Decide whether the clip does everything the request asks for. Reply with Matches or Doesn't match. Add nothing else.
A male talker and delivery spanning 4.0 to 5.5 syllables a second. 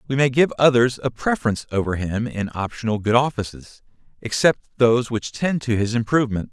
Doesn't match